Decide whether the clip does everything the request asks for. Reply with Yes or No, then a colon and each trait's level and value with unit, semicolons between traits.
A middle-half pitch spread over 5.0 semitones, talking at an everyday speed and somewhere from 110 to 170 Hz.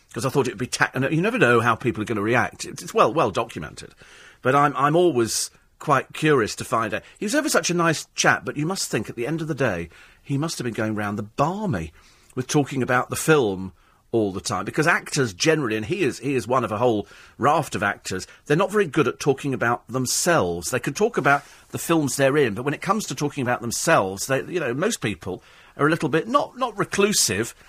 No: wide, 5.4 semitones; fast, 245 wpm; low, 135 Hz